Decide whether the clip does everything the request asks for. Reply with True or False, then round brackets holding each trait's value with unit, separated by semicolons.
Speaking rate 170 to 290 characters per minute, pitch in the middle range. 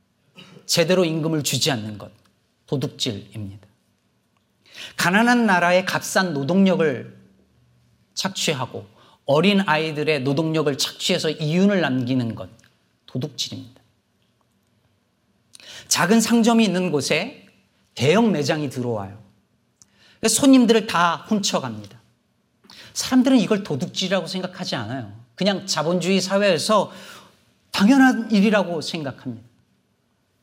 True (255 characters per minute; 160 Hz)